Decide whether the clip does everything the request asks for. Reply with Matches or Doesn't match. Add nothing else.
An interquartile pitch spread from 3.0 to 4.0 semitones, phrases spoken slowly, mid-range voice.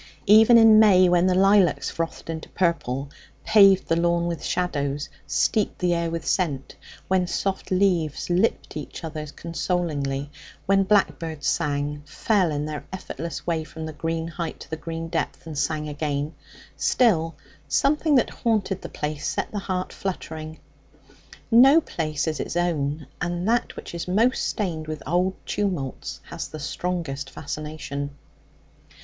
Doesn't match